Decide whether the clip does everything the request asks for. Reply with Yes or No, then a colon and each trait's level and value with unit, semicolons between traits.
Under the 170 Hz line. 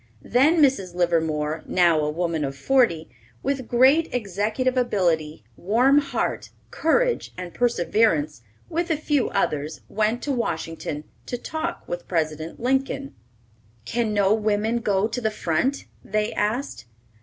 No: high, 215 Hz